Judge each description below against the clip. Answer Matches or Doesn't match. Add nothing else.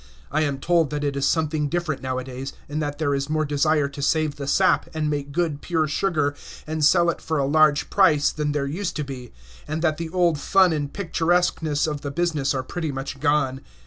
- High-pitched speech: Doesn't match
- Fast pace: Matches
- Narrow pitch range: Matches